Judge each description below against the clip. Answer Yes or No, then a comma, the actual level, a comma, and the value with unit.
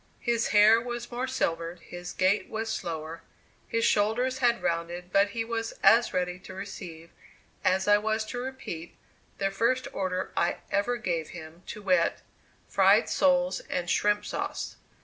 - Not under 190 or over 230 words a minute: No, average, 155 wpm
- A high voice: Yes, high, 205 Hz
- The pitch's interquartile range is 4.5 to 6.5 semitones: Yes, average, 4.8 semitones